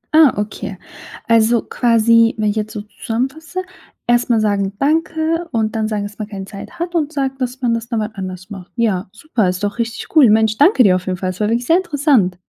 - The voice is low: No, high, 225 Hz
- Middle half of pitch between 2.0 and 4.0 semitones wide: No, average, 4.6 semitones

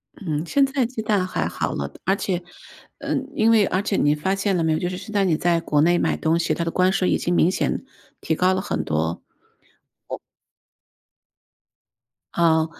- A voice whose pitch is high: No, medium, 180 Hz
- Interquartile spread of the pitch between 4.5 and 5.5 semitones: No, average, 3.6 semitones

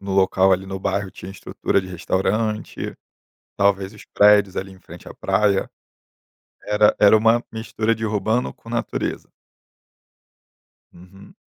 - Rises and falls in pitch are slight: Yes, narrow, 2.1 semitones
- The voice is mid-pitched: No, low, 100 Hz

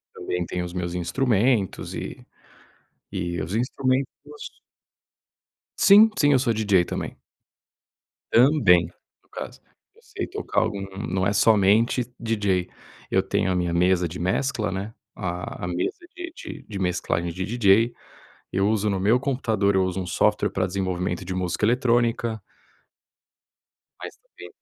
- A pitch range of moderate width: Yes, average, 4.3 semitones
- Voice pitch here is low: Yes, low, 100 Hz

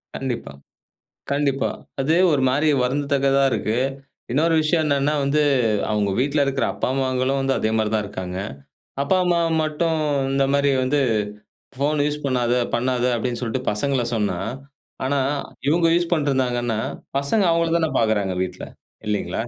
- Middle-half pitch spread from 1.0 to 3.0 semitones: No, average, 3.4 semitones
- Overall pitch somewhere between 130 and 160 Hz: Yes, low, 135 Hz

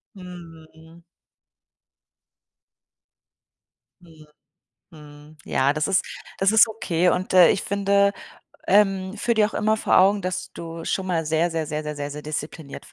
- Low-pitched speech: No, medium, 175 Hz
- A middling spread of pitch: Yes, average, 3.9 semitones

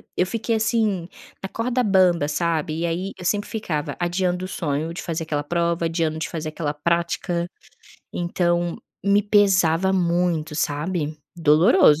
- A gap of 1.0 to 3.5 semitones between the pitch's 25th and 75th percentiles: Yes, average, 3.0 semitones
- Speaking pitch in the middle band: Yes, medium, 170 Hz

